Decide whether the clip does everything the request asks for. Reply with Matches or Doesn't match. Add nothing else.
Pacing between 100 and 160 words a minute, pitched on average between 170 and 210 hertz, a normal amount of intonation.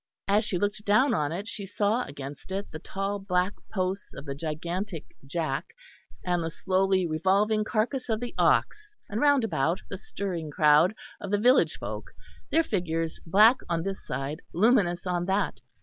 Doesn't match